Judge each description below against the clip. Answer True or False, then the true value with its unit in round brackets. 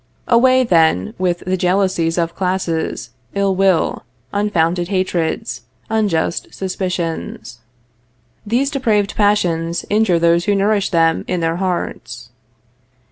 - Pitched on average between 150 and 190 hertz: True (185 Hz)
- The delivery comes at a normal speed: False (110 wpm)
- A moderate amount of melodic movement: True (3.5 semitones)